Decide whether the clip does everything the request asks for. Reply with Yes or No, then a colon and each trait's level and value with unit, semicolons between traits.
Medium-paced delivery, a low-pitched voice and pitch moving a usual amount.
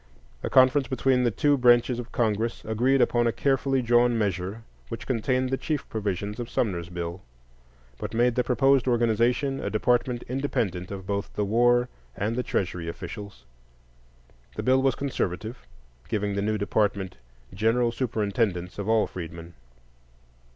Yes: average, 150 wpm; low, 115 Hz; average, 3.8 semitones